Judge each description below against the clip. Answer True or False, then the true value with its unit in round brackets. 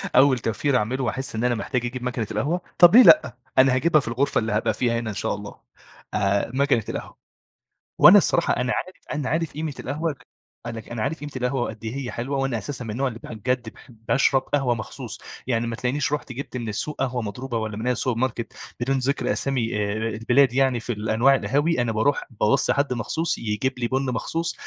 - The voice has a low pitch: True (125 Hz)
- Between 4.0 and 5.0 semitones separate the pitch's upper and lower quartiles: False (3.3 semitones)